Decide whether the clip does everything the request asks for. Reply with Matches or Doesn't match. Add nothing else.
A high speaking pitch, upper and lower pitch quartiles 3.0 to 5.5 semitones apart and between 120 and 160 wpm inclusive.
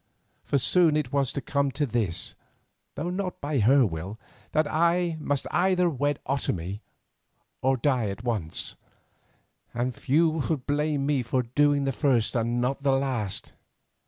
Doesn't match